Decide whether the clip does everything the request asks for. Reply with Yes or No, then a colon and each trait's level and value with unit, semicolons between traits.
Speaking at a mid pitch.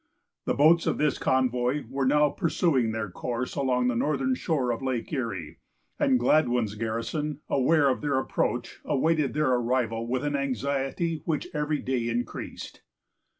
No: low, 130 Hz